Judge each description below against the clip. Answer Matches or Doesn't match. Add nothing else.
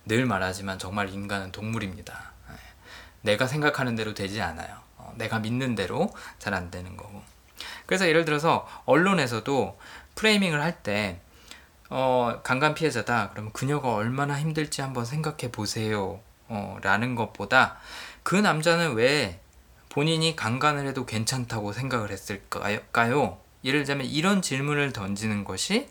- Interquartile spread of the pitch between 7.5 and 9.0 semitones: Doesn't match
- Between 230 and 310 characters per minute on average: Matches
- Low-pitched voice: Matches